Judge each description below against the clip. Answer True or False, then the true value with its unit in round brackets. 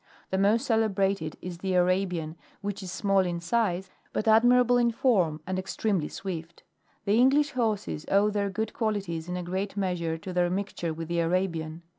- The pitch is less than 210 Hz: True (190 Hz)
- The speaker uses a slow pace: False (170 wpm)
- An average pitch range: True (3.5 semitones)